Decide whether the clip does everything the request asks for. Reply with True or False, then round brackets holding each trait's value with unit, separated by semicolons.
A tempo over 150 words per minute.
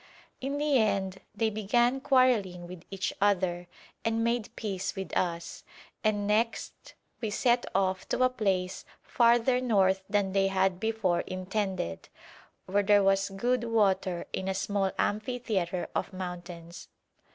False (140 wpm)